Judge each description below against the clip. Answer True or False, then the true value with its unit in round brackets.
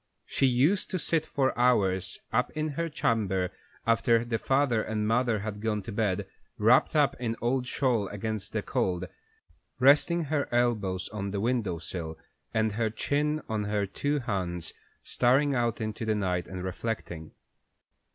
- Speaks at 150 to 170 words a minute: True (160 wpm)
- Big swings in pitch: False (4.3 semitones)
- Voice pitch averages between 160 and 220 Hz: False (115 Hz)